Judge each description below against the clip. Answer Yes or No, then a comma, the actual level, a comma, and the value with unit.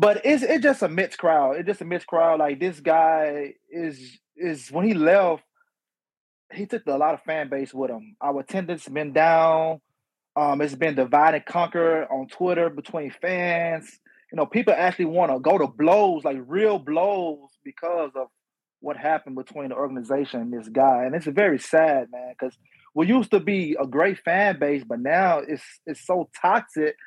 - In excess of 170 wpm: Yes, average, 190 wpm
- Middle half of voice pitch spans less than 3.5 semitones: No, average, 4.2 semitones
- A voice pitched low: No, medium, 160 Hz